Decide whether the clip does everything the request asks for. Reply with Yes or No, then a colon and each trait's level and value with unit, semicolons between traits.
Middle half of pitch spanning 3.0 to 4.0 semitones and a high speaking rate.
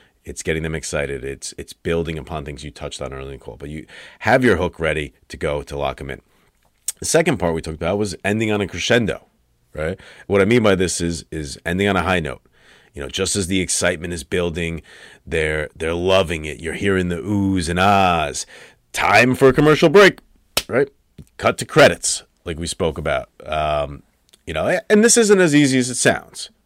No: average, 4.4 semitones; fast, 210 wpm